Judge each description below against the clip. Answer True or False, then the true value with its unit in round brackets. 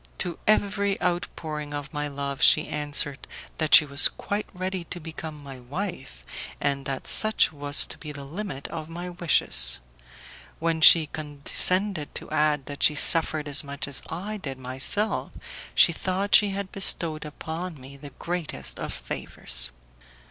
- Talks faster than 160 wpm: False (155 wpm)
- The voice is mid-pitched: True (155 Hz)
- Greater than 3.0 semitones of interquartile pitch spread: True (4.0 semitones)